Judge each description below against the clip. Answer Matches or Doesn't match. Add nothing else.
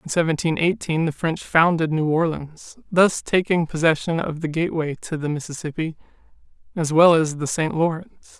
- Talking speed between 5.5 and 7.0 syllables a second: Doesn't match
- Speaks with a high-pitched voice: Doesn't match